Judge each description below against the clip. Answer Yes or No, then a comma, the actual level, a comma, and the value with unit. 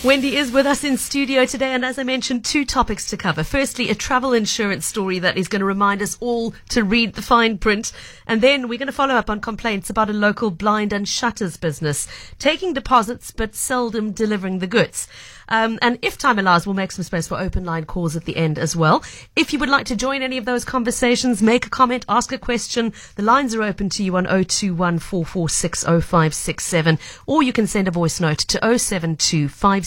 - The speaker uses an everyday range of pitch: Yes, average, 5.0 semitones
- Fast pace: Yes, fast, 235 wpm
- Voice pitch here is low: No, high, 220 Hz